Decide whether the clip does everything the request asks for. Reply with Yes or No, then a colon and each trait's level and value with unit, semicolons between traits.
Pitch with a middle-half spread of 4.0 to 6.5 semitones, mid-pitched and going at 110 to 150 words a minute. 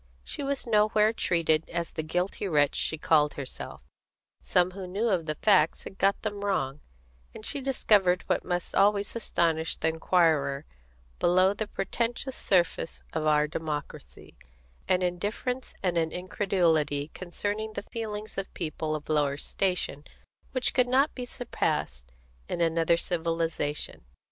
Yes: average, 4.7 semitones; medium, 180 Hz; average, 145 wpm